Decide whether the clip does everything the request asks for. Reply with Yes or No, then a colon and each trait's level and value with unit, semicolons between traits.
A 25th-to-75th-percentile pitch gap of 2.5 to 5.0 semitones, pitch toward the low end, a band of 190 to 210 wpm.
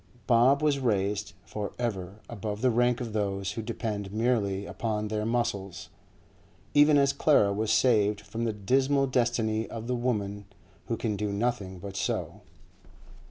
No: average, 3.2 semitones; low, 110 Hz; average, 155 wpm